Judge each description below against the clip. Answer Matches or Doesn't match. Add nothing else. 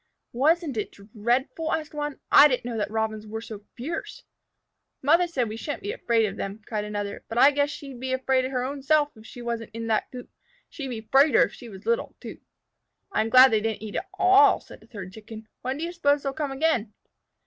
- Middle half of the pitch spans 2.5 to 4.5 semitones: Doesn't match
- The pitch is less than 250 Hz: Doesn't match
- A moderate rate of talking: Doesn't match